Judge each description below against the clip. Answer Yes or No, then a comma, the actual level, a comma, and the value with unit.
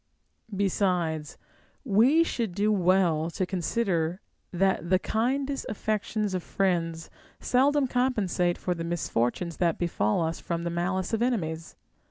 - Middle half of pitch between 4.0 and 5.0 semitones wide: Yes, average, 4.3 semitones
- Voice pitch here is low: No, medium, 185 Hz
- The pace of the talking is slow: Yes, slow, 130 wpm